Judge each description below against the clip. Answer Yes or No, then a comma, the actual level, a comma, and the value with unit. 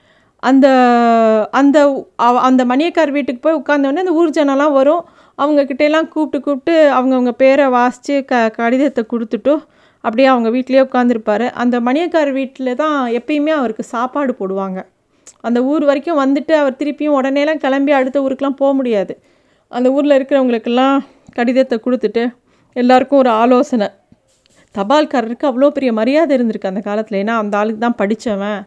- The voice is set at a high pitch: Yes, very high, 265 Hz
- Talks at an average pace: No, fast, 135 wpm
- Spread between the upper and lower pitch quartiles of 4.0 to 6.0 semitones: No, average, 3.2 semitones